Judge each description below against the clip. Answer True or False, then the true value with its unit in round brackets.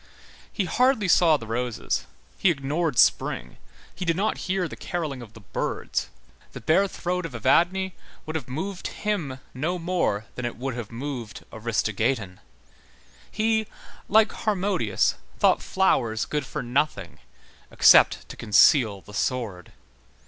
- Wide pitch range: True (7.9 semitones)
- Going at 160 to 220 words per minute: False (140 wpm)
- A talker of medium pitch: True (145 Hz)